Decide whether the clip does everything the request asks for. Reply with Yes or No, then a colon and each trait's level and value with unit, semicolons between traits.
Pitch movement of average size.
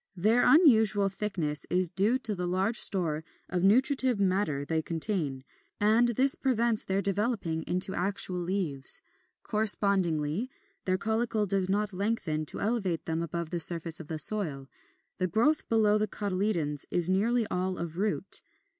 Yes: average, 4.2 semitones